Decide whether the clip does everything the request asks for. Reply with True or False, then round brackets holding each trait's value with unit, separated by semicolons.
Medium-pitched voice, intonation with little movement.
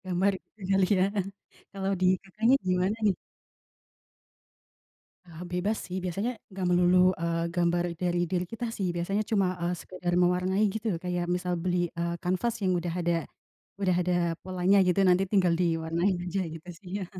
True (180 Hz; 1.8 semitones)